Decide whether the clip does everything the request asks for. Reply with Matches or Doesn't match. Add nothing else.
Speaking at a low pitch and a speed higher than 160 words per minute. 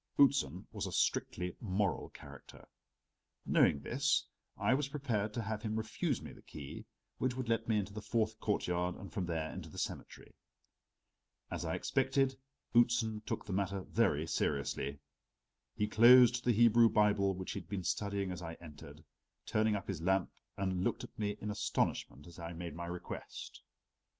Matches